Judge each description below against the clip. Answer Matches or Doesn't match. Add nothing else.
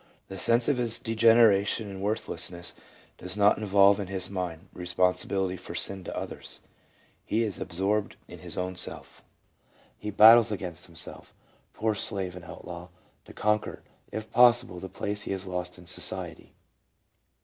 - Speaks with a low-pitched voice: Matches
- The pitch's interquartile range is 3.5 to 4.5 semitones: Doesn't match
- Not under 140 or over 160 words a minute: Matches